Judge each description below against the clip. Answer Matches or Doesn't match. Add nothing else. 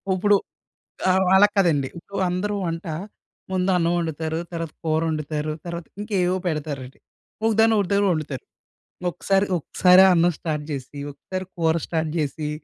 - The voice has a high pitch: Doesn't match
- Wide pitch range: Doesn't match